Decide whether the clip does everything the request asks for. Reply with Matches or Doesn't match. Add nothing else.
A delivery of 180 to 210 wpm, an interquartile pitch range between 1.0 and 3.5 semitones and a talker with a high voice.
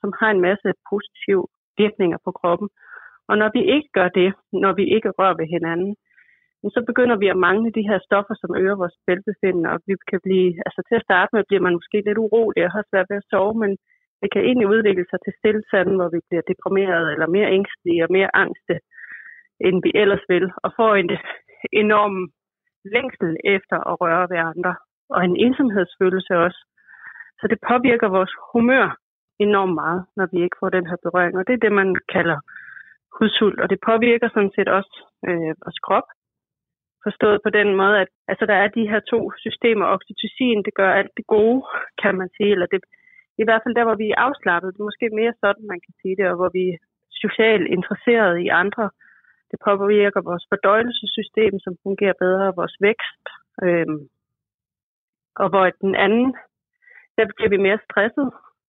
Matches